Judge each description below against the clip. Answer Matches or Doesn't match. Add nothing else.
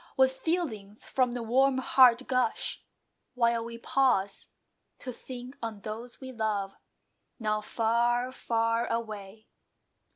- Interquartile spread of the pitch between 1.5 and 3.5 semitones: Matches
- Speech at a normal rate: Doesn't match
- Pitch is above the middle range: Matches